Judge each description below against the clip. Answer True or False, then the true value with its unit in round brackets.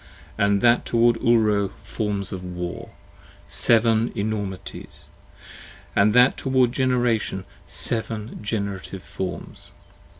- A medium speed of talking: False (95 wpm)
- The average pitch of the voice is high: False (110 Hz)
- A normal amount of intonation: True (3.0 semitones)